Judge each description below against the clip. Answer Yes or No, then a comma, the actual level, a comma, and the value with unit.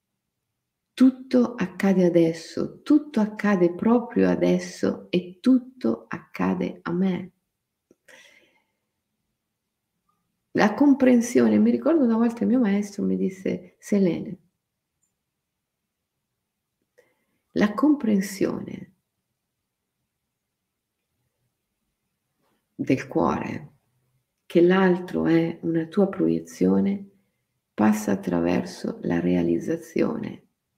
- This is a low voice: No, medium, 180 Hz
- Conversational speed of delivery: No, slow, 75 wpm